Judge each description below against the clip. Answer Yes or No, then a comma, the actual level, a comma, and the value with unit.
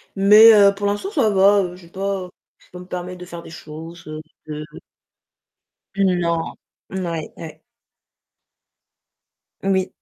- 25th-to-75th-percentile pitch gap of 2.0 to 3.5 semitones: Yes, average, 2.8 semitones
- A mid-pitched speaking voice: Yes, medium, 180 Hz